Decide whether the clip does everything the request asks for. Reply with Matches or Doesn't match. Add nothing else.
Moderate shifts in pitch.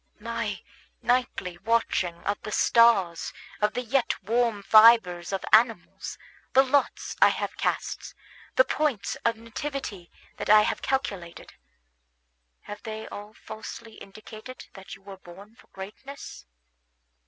Matches